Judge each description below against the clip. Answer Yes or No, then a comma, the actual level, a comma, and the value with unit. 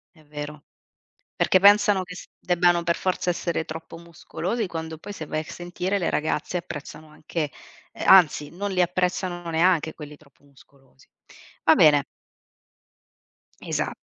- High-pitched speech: No, medium, 170 Hz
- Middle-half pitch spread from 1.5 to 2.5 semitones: No, average, 2.9 semitones